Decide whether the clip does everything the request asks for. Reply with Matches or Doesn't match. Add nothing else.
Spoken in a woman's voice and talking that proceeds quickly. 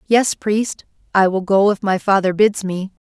Doesn't match